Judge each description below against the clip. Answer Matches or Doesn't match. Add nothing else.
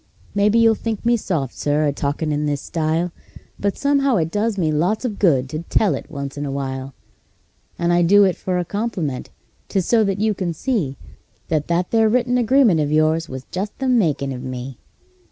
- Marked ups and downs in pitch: Matches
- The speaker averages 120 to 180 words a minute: Doesn't match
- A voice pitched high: Doesn't match